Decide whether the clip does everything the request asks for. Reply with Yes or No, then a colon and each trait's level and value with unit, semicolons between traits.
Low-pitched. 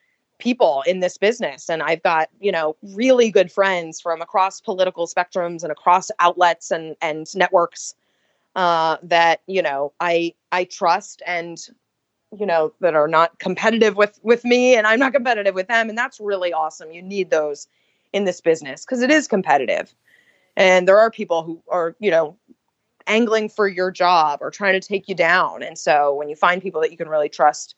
No: medium, 180 Hz